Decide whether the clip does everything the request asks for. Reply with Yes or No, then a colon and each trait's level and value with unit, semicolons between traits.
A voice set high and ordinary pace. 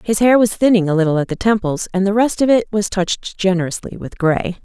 No: high, 195 Hz; fast, 245 wpm